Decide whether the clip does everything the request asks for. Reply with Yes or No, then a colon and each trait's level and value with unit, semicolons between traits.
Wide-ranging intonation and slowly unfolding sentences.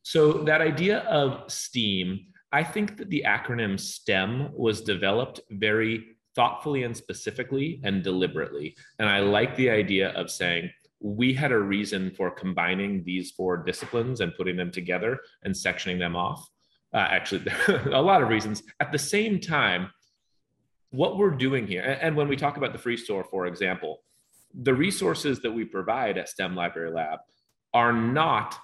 No: wide, 6.7 semitones; average, 165 wpm